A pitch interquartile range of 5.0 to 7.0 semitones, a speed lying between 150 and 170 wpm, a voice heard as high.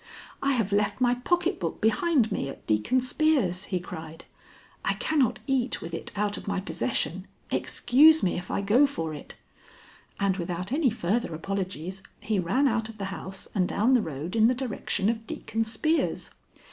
No: wide, 5.6 semitones; average, 180 wpm; high, 210 Hz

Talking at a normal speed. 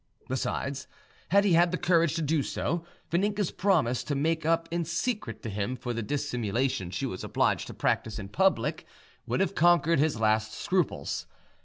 Yes: average, 175 wpm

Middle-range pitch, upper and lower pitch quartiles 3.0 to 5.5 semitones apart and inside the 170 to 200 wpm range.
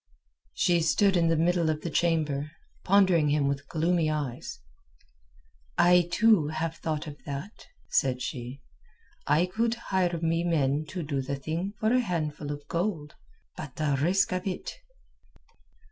No: medium, 165 Hz; average, 3.4 semitones; average, 150 wpm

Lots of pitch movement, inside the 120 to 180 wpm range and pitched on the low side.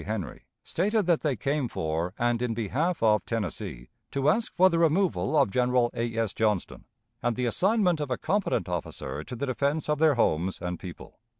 No: wide, 6.9 semitones; average, 190 wpm; low, 125 Hz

